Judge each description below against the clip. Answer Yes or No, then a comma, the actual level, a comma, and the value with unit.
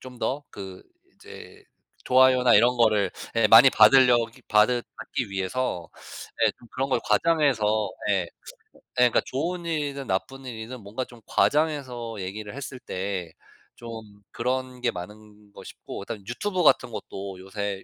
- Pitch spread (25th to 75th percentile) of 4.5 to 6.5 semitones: No, average, 4.0 semitones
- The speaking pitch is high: No, low, 120 Hz